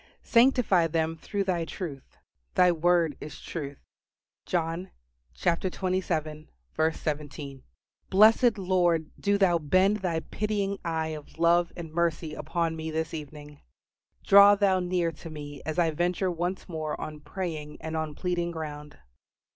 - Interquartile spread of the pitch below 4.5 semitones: Yes, average, 2.9 semitones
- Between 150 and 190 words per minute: No, slow, 135 wpm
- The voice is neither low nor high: Yes, medium, 165 Hz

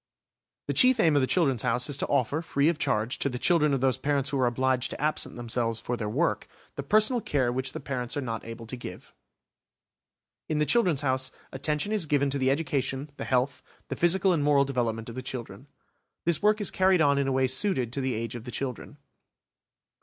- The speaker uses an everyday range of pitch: Yes, average, 3.4 semitones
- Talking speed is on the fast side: Yes, fast, 220 wpm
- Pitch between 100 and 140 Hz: Yes, low, 135 Hz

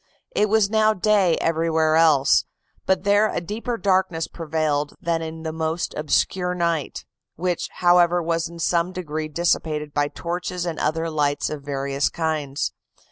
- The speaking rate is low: No, average, 150 wpm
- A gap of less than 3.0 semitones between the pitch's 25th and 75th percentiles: Yes, narrow, 2.4 semitones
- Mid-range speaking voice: Yes, medium, 165 Hz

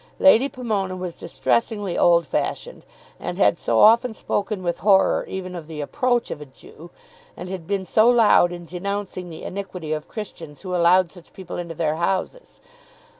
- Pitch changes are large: No, average, 3.7 semitones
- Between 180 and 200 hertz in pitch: Yes, medium, 185 Hz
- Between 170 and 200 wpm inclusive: Yes, average, 175 wpm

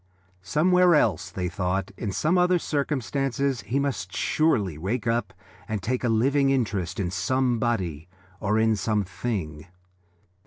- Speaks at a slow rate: Yes, slow, 130 wpm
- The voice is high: No, low, 110 Hz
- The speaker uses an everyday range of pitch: No, wide, 6.5 semitones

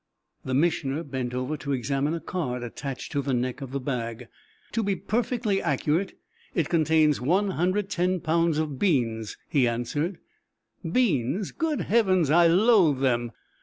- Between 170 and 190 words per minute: No, average, 145 wpm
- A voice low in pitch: No, medium, 155 Hz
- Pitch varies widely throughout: Yes, wide, 6.1 semitones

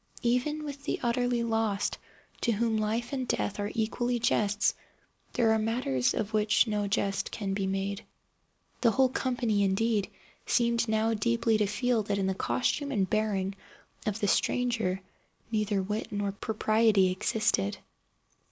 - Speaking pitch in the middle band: No, high, 215 Hz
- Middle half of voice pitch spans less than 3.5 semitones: Yes, average, 2.8 semitones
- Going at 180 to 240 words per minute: No, average, 150 wpm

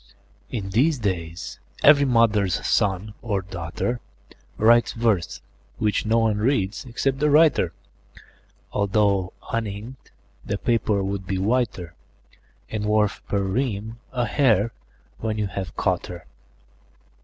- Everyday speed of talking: No, slow, 120 wpm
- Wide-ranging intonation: No, average, 3.4 semitones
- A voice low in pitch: Yes, low, 105 Hz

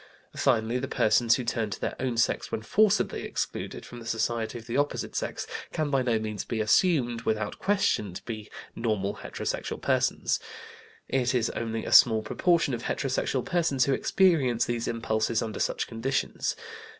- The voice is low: Yes, low, 120 Hz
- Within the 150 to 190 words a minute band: Yes, average, 170 wpm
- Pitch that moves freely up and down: No, average, 3.3 semitones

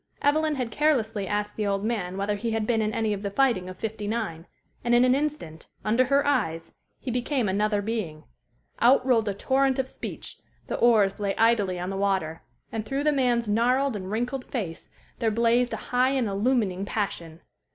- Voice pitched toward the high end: Yes, high, 225 Hz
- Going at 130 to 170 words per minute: No, average, 195 wpm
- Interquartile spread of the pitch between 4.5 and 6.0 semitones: No, average, 4.1 semitones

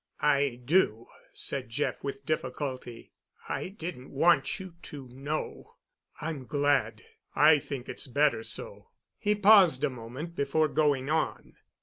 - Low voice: No, medium, 145 Hz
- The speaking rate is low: Yes, slow, 130 wpm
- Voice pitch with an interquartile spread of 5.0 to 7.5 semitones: No, average, 3.6 semitones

